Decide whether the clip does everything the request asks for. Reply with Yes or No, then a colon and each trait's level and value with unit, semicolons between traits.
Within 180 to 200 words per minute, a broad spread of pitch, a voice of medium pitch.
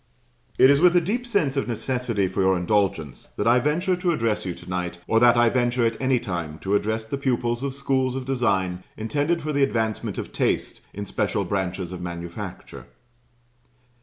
No: average, 190 wpm; wide, 6.2 semitones; low, 120 Hz